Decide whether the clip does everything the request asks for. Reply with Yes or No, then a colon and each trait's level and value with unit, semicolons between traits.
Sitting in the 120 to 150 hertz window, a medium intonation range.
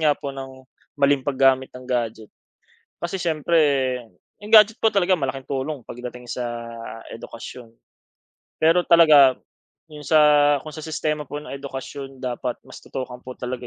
Yes: medium, 140 Hz; average, 3.3 semitones